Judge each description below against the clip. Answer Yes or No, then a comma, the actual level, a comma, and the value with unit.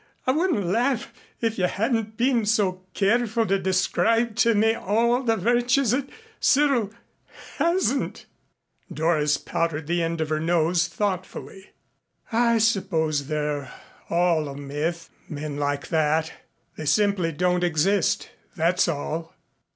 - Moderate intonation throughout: No, wide, 6.1 semitones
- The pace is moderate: No, slow, 130 wpm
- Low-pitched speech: No, medium, 185 Hz